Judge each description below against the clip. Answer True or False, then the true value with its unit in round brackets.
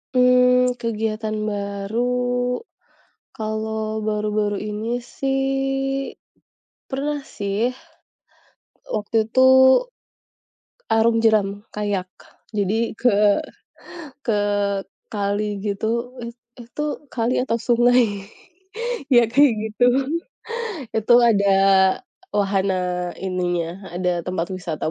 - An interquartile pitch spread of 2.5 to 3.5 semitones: True (2.9 semitones)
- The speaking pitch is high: True (215 Hz)